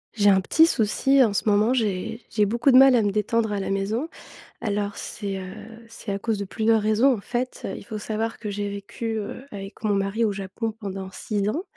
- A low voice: No, high, 210 Hz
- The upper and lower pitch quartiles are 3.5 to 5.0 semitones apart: No, narrow, 2.4 semitones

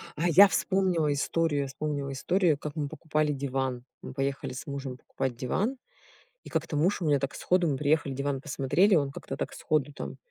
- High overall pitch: No, medium, 145 Hz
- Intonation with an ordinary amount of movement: Yes, average, 3.0 semitones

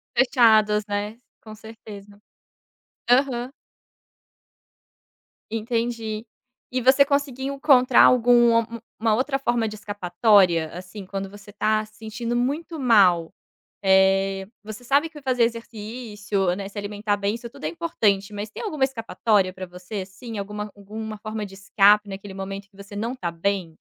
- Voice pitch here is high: Yes, high, 215 Hz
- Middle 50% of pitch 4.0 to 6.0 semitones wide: No, average, 3.3 semitones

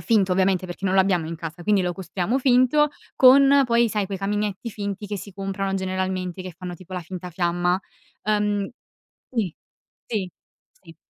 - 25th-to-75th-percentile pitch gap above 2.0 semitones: Yes, narrow, 2.5 semitones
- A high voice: Yes, high, 195 Hz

